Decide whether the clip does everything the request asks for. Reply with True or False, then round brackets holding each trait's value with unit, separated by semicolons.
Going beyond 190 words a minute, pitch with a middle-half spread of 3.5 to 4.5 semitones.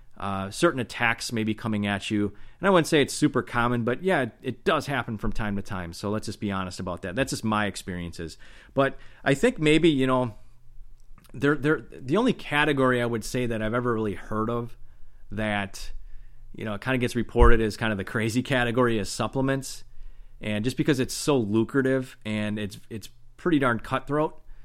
True (200 wpm; 4.0 semitones)